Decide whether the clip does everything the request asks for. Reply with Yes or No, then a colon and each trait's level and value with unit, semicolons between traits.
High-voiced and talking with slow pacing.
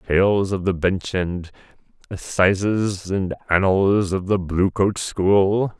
No: very low, 95 Hz; slow, 125 wpm